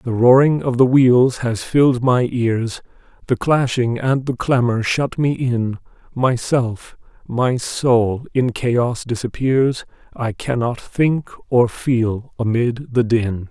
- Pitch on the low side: Yes, low, 125 Hz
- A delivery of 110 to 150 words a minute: Yes, average, 140 wpm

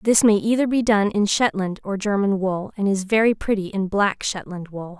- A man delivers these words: No, female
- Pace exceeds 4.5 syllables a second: Yes, 4.9 syllables/s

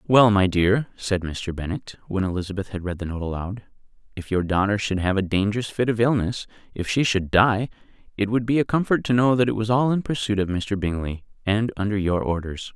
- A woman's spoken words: No, male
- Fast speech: Yes, fast, 215 wpm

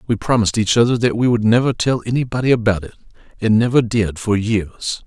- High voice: No, low, 110 Hz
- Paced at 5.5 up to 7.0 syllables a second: Yes, 5.9 syllables/s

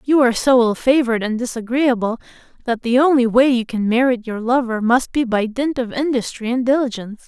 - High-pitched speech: Yes, high, 245 Hz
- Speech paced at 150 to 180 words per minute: No, average, 200 wpm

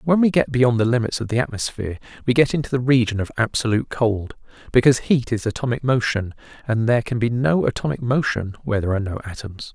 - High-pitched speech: No, low, 120 Hz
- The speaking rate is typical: No, fast, 210 wpm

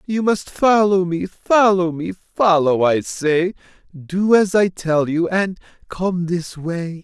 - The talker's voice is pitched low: No, medium, 180 Hz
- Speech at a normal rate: Yes, average, 155 wpm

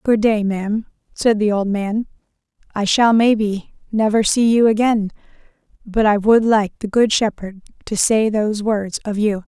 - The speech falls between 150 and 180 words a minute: Yes, average, 170 wpm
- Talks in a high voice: Yes, high, 215 Hz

